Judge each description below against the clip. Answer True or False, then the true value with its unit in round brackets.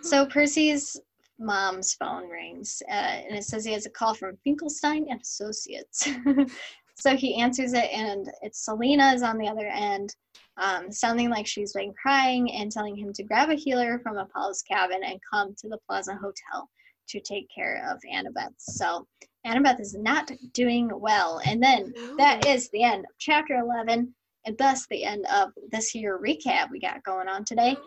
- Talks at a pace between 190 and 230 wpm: False (180 wpm)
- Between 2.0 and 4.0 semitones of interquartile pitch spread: False (4.8 semitones)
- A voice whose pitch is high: True (235 Hz)